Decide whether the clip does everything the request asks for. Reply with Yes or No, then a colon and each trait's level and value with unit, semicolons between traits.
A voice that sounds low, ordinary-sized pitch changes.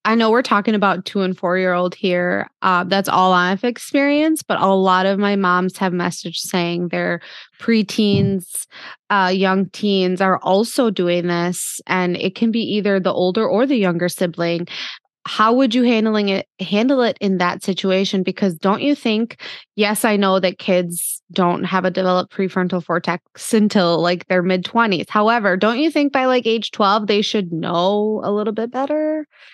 No: high, 195 Hz; average, 3.2 semitones